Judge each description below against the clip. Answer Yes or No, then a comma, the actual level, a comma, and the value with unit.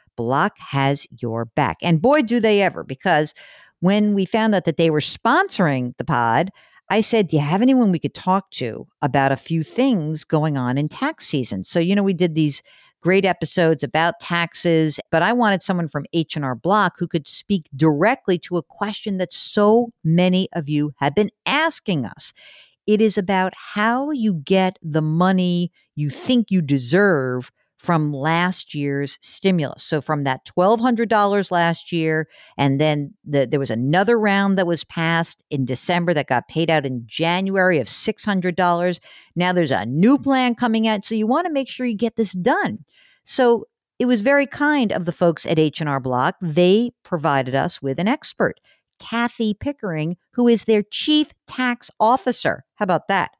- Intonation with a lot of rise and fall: Yes, wide, 5.7 semitones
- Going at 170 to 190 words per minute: Yes, average, 180 wpm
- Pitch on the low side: No, medium, 175 Hz